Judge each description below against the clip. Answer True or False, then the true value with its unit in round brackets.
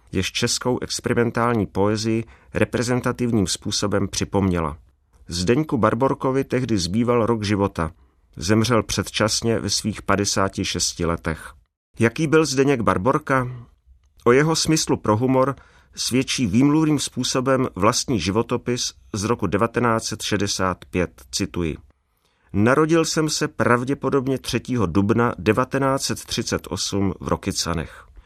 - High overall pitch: False (110 Hz)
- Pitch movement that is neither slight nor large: True (4.9 semitones)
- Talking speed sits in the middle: False (100 wpm)